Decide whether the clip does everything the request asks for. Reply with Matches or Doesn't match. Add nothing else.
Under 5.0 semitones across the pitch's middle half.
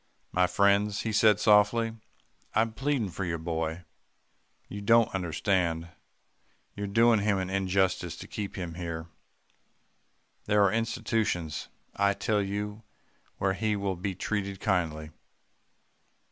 Matches